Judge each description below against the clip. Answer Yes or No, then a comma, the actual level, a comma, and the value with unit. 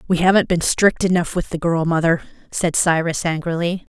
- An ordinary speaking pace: Yes, average, 180 wpm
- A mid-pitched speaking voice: Yes, medium, 170 Hz